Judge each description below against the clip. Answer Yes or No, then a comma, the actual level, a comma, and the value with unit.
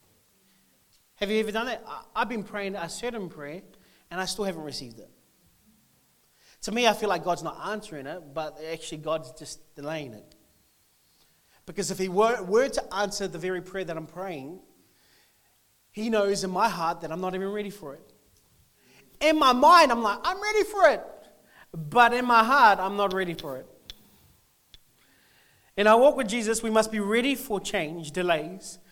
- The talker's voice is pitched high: Yes, high, 195 Hz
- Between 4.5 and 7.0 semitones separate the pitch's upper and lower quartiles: Yes, average, 5.3 semitones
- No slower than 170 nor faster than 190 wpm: Yes, average, 180 wpm